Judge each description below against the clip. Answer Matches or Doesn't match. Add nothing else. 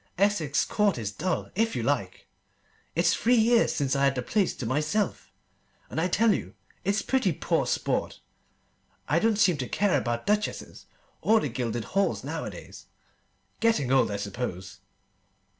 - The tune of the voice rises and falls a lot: Matches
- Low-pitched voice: Doesn't match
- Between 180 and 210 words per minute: Doesn't match